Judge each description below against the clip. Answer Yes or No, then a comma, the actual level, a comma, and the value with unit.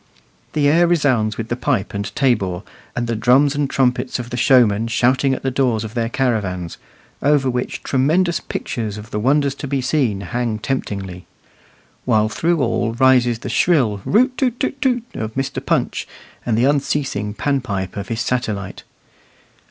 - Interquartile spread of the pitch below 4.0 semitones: No, average, 4.4 semitones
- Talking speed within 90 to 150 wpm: No, average, 175 wpm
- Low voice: Yes, low, 125 Hz